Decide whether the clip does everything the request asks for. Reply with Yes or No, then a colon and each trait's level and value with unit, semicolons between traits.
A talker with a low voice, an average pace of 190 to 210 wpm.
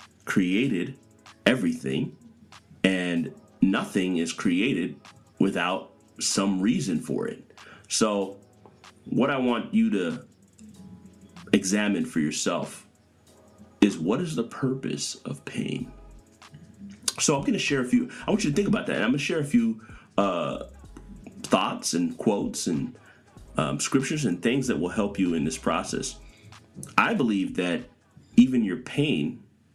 No: low, 120 Hz; average, 140 wpm